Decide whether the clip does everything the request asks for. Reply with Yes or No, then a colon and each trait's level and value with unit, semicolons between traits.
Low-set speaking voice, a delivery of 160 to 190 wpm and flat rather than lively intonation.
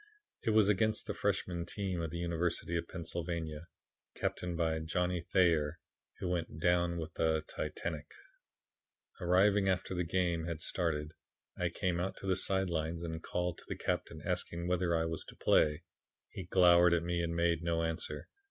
Yes: very low, 85 Hz; average, 170 wpm; narrow, 1.4 semitones